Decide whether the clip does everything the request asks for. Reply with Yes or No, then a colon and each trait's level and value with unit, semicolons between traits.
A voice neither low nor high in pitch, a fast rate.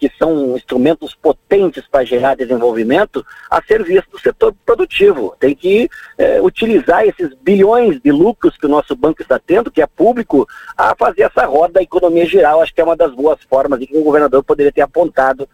Yes: medium, 170 Hz; fast, 195 wpm